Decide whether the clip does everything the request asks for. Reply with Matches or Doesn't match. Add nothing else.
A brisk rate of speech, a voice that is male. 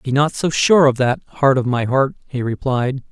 Matches